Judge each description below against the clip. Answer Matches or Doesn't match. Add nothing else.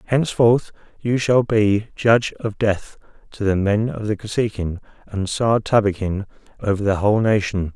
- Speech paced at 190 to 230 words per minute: Doesn't match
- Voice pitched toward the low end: Matches